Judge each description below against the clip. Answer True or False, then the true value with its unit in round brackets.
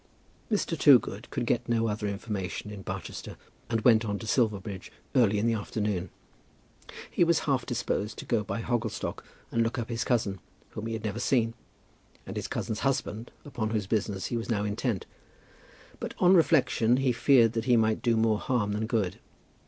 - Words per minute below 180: False (185 wpm)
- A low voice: True (115 Hz)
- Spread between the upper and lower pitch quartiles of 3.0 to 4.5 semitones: False (2.6 semitones)